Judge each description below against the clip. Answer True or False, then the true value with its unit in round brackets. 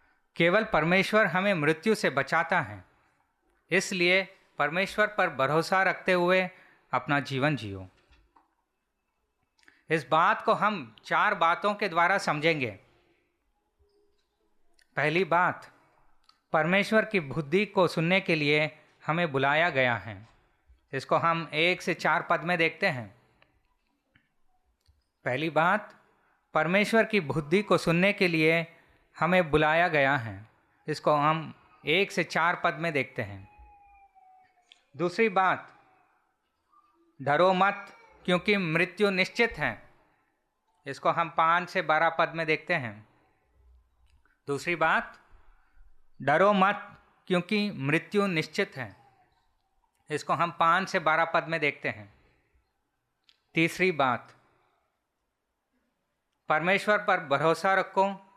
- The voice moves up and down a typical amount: True (4.2 semitones)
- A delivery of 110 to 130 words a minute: True (115 wpm)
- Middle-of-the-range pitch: True (170 Hz)